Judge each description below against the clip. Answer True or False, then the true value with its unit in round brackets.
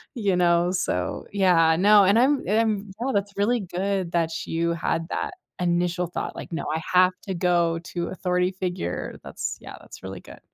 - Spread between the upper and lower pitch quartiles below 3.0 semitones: True (2.6 semitones)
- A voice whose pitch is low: False (180 Hz)